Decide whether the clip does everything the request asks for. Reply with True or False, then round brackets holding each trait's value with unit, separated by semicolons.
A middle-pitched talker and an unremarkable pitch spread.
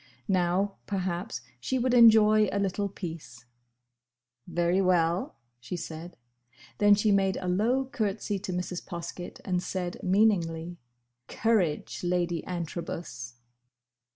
True (180 Hz; 3.0 semitones)